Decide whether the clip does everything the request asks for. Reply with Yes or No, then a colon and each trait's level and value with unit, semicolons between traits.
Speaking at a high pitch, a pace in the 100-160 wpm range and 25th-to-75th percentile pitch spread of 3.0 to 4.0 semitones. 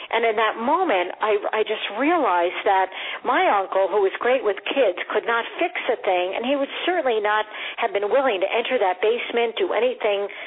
No: high, 215 Hz; average, 200 wpm; average, 3.6 semitones